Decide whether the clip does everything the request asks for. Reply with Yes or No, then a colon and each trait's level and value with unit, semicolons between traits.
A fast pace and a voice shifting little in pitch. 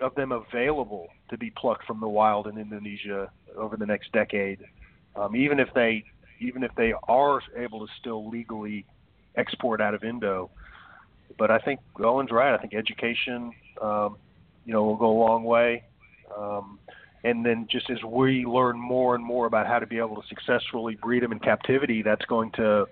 No: average, 185 wpm; narrow, 2.3 semitones